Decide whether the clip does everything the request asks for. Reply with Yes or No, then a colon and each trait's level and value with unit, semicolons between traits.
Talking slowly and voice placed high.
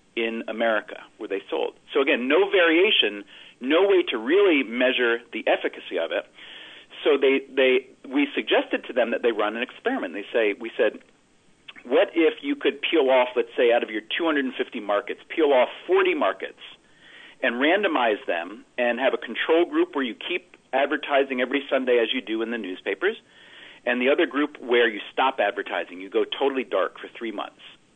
No: average, 185 wpm; high, 230 Hz